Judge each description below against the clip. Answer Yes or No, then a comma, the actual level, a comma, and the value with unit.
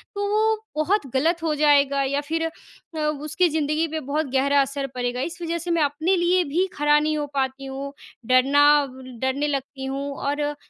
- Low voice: No, very high, 290 Hz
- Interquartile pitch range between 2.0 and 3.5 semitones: Yes, average, 2.9 semitones